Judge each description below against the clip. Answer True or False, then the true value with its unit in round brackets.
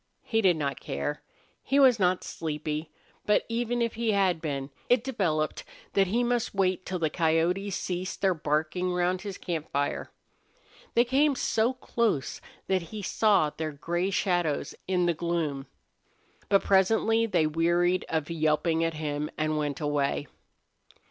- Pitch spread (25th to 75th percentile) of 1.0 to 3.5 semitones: False (4.7 semitones)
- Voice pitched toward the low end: False (175 Hz)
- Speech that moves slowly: False (155 wpm)